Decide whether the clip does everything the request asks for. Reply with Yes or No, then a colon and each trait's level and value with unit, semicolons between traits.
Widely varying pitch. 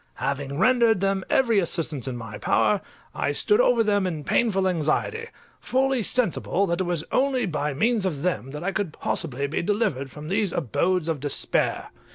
Yes: wide, 6.6 semitones